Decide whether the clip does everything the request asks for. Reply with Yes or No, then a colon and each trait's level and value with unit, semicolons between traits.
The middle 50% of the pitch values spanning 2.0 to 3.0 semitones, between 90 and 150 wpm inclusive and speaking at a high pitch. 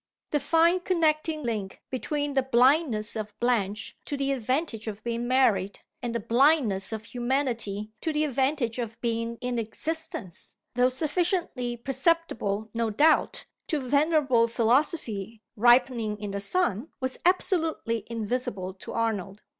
No: average, 4.9 semitones; slow, 135 wpm; high, 245 Hz